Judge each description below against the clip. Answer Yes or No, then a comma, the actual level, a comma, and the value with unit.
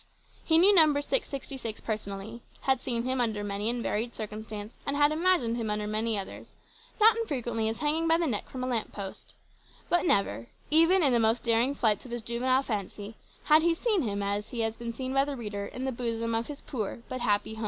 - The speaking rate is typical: No, fast, 215 wpm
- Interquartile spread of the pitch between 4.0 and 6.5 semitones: Yes, average, 4.6 semitones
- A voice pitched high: Yes, high, 235 Hz